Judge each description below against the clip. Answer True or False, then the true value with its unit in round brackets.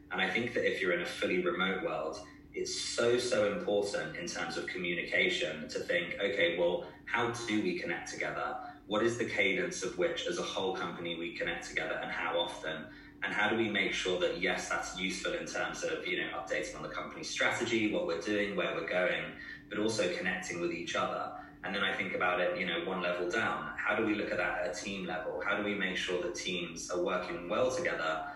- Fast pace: True (230 wpm)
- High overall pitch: False (105 Hz)